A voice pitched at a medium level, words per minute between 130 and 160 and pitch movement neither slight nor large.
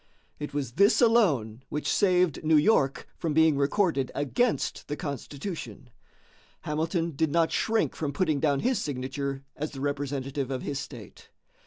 Yes: medium, 145 Hz; average, 150 wpm; average, 3.4 semitones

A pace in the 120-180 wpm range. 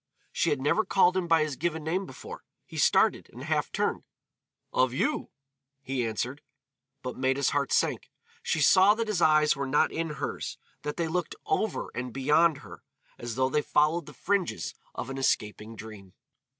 Yes: average, 175 wpm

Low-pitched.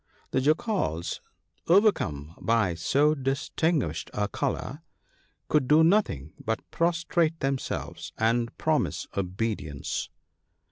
Yes: low, 130 Hz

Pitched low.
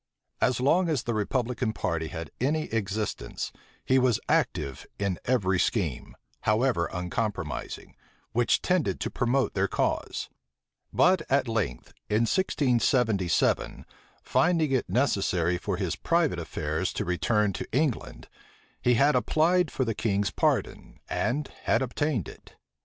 Yes: low, 120 Hz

